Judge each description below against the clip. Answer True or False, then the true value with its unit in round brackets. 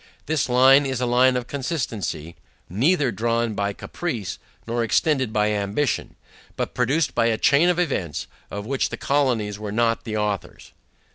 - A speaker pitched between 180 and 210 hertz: False (120 Hz)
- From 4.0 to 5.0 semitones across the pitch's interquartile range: True (4.5 semitones)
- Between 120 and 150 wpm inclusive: False (160 wpm)